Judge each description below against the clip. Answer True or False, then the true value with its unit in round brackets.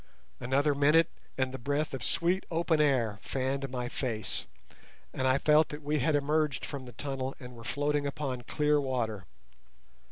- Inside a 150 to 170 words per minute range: True (165 wpm)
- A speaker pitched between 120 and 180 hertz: True (140 Hz)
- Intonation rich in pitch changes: False (2.6 semitones)